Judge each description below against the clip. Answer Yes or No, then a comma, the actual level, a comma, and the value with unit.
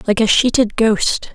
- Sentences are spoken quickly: No, average, 180 wpm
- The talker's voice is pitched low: No, high, 225 Hz